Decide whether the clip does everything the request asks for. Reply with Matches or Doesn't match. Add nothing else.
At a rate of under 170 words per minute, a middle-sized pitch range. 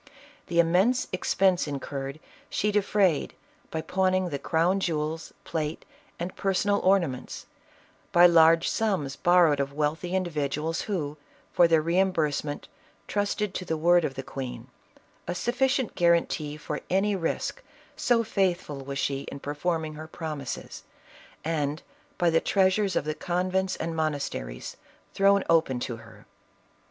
Matches